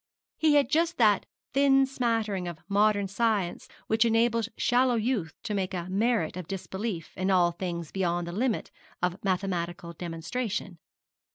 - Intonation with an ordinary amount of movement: Yes, average, 4.8 semitones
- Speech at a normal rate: Yes, average, 150 wpm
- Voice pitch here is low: No, high, 200 Hz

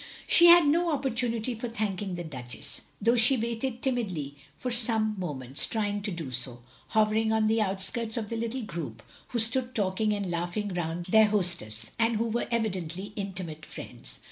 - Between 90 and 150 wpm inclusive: No, average, 180 wpm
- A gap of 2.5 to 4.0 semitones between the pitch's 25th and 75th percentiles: No, average, 4.8 semitones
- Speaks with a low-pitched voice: No, high, 215 Hz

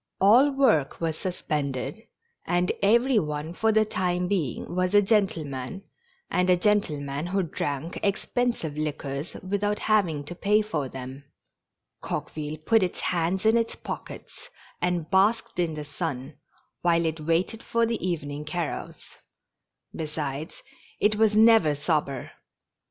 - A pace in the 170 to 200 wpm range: No, average, 145 wpm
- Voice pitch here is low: No, medium, 175 Hz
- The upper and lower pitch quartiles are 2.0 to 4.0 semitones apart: No, wide, 5.6 semitones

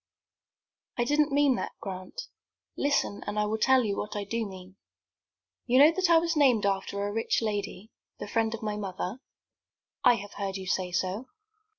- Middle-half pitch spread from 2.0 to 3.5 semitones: No, average, 4.5 semitones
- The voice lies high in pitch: Yes, high, 215 Hz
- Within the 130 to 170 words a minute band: No, average, 185 wpm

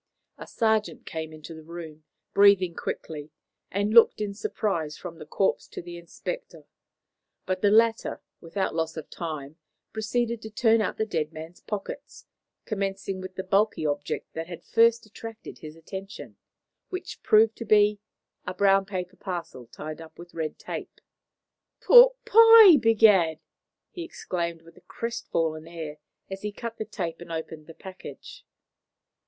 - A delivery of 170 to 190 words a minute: No, average, 155 wpm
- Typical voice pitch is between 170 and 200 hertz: Yes, high, 190 Hz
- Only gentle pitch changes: No, average, 4.9 semitones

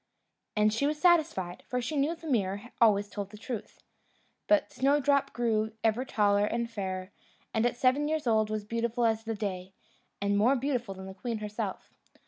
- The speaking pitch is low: No, high, 225 Hz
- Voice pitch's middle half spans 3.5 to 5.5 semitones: Yes, average, 4.0 semitones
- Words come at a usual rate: Yes, average, 180 wpm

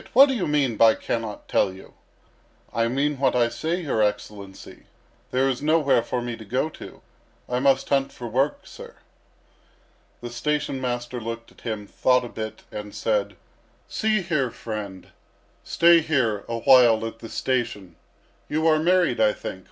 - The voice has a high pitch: No, low, 125 Hz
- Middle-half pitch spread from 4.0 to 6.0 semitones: Yes, average, 4.8 semitones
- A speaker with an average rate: Yes, average, 165 wpm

